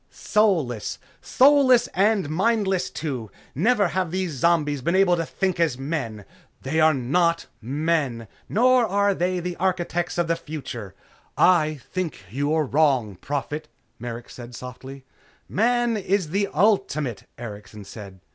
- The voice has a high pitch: No, medium, 160 Hz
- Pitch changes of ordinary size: No, wide, 6.4 semitones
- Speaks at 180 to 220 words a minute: No, slow, 135 wpm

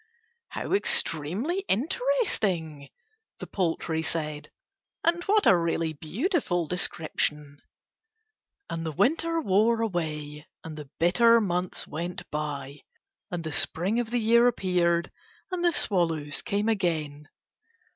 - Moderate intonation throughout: No, wide, 6.9 semitones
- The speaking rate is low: Yes, slow, 115 wpm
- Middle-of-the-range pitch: Yes, medium, 175 Hz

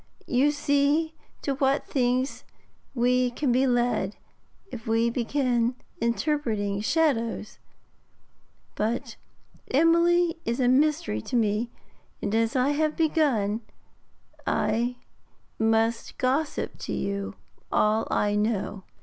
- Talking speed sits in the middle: No, slow, 105 wpm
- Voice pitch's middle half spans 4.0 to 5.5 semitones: Yes, average, 4.3 semitones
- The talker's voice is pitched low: No, high, 245 Hz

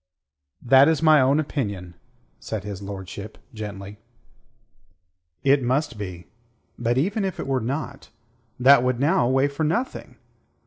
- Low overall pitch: Yes, low, 130 Hz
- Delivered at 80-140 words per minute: Yes, slow, 135 wpm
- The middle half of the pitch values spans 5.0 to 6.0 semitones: Yes, wide, 5.6 semitones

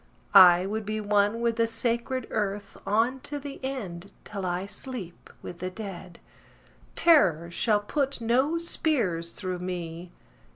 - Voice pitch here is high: Yes, high, 210 Hz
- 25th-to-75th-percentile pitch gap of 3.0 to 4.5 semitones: No, average, 5.2 semitones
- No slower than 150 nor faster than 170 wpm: No, average, 140 wpm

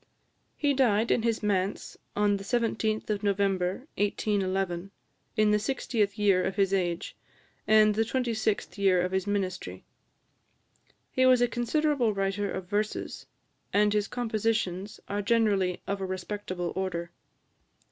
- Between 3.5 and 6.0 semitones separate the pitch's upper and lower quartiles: No, narrow, 2.6 semitones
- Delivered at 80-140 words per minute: Yes, slow, 135 wpm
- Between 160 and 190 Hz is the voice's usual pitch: No, high, 205 Hz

